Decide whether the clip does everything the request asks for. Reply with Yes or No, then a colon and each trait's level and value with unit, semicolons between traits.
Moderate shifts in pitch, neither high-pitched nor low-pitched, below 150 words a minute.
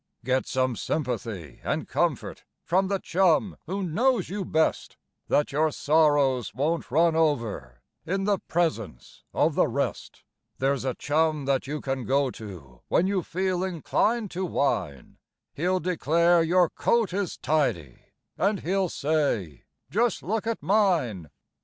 No: wide, 6.1 semitones; medium, 160 Hz; average, 140 wpm